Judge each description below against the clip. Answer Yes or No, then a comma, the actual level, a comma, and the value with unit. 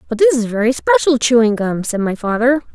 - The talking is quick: Yes, fast, 220 wpm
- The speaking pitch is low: No, high, 245 Hz